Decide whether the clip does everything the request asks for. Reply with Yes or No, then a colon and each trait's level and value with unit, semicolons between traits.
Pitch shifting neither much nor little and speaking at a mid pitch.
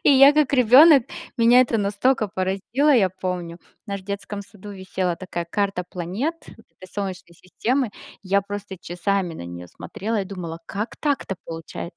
No: average, 4.1 semitones; high, 200 Hz